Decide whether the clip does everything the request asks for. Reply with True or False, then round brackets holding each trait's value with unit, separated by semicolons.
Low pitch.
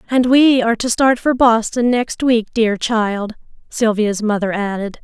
False (230 Hz)